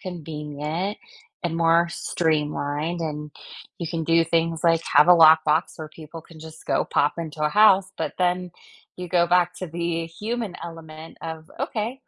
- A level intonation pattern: Yes, narrow, 2.0 semitones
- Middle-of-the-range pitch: Yes, medium, 165 Hz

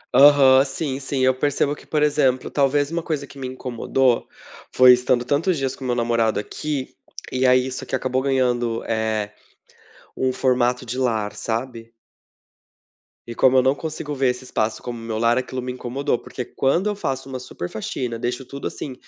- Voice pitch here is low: Yes, low, 130 Hz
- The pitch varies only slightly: Yes, narrow, 2.1 semitones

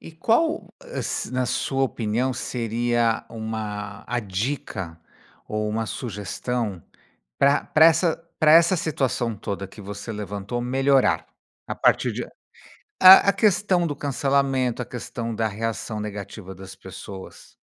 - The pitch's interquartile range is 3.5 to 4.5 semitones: No, average, 5.2 semitones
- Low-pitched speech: Yes, low, 120 Hz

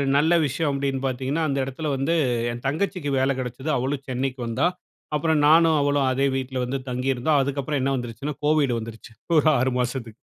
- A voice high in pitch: No, low, 135 Hz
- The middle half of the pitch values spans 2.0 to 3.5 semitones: Yes, narrow, 2.5 semitones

